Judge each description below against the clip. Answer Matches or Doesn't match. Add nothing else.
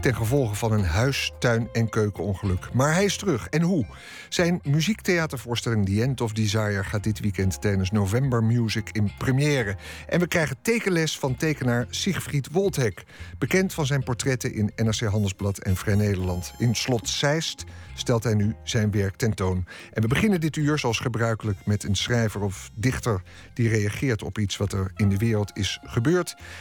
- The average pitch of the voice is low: Matches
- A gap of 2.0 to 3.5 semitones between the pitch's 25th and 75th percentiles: Doesn't match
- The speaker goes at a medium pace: Matches